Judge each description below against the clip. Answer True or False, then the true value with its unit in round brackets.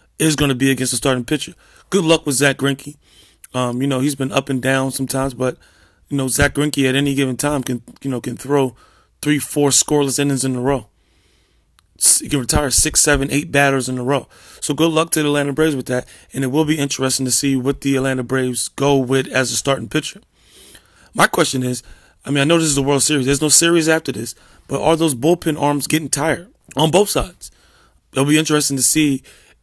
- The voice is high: False (140 Hz)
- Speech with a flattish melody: True (2.2 semitones)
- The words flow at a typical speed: False (225 wpm)